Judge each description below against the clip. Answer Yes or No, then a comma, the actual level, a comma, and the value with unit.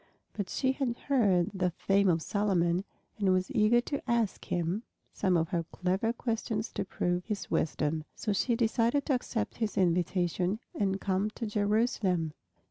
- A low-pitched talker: No, high, 200 Hz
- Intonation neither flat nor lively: Yes, average, 4.1 semitones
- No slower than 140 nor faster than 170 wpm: Yes, average, 160 wpm